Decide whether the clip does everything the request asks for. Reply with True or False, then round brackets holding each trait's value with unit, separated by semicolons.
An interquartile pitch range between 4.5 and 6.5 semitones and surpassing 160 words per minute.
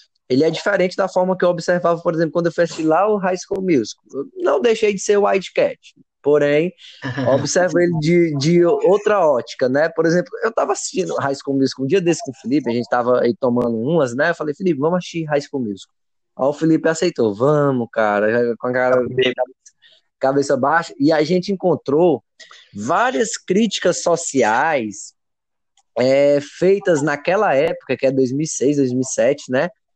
True (5.1 semitones; 180 wpm)